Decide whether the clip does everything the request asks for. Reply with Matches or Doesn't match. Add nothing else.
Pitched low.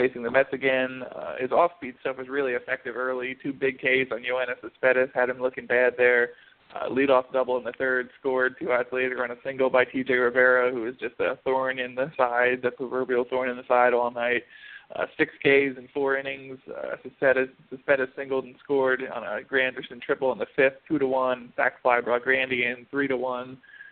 Matches